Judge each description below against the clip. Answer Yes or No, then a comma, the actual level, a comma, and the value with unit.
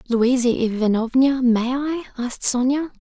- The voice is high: Yes, very high, 250 Hz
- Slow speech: Yes, slow, 120 wpm